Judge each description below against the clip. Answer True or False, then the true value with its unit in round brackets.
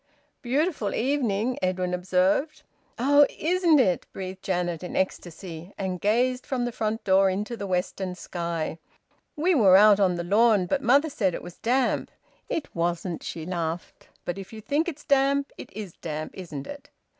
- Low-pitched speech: False (200 Hz)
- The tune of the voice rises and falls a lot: True (6.2 semitones)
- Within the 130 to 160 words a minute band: False (170 wpm)